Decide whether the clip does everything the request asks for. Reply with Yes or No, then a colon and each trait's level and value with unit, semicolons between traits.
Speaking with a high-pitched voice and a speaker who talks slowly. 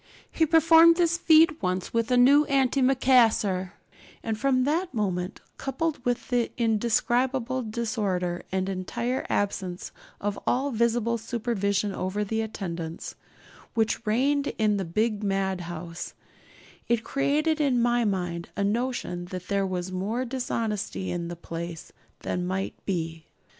Yes: high, 220 Hz; slow, 130 wpm